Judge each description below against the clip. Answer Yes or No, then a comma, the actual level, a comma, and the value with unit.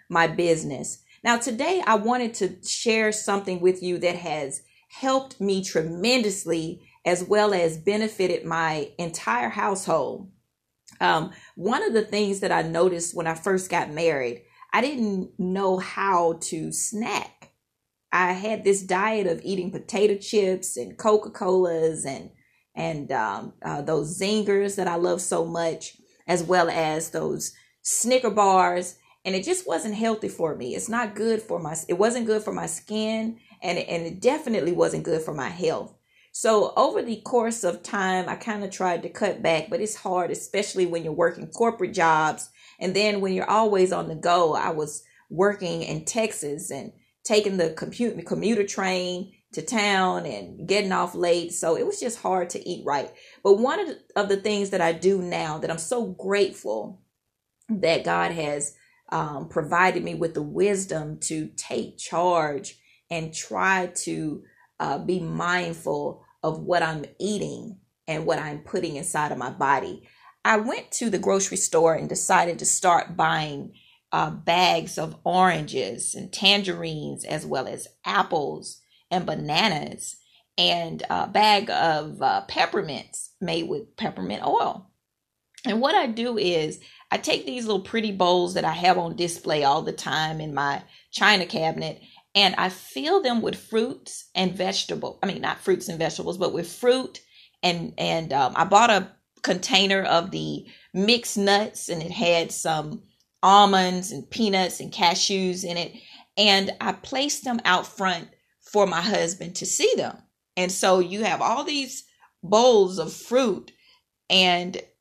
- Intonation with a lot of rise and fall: No, average, 3.9 semitones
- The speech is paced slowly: No, average, 165 wpm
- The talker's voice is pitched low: No, medium, 185 Hz